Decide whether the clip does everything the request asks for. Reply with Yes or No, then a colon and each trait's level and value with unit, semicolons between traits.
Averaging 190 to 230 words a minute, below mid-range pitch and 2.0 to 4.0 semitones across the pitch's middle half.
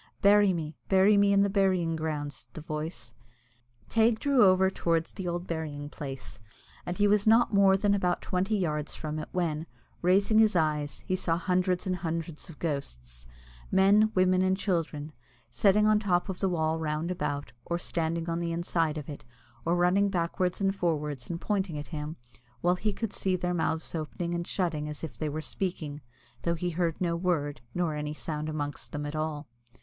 No: average, 195 wpm; medium, 170 Hz; average, 3.6 semitones